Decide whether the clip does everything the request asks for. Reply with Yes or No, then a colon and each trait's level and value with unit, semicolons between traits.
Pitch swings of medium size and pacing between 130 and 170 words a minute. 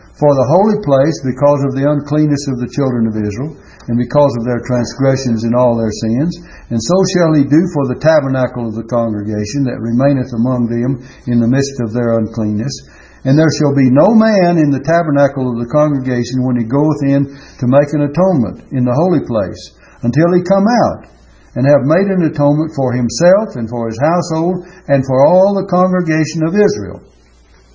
No: average, 4.6 semitones; average, 190 wpm